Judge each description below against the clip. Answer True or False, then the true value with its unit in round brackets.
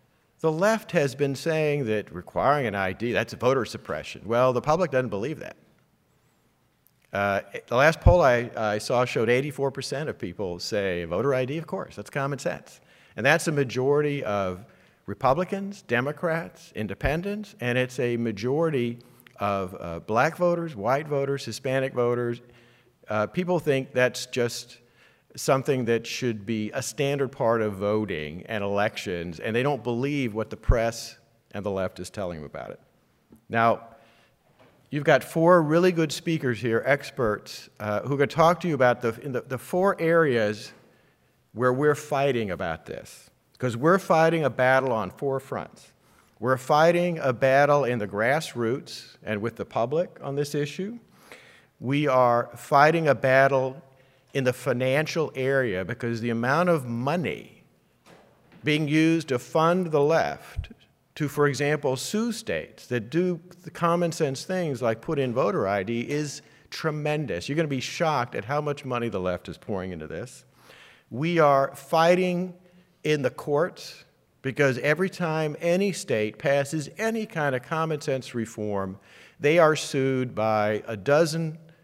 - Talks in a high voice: False (135 Hz)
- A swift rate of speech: False (160 wpm)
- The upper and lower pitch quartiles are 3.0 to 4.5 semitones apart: False (5.0 semitones)